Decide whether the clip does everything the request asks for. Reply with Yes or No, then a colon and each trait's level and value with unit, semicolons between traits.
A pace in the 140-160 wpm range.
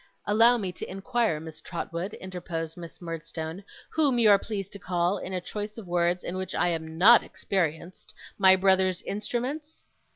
No: average, 170 wpm